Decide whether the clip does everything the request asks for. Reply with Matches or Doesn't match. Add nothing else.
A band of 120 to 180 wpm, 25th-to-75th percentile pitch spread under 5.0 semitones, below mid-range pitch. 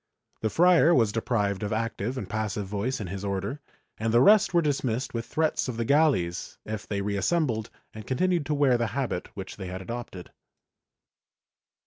Doesn't match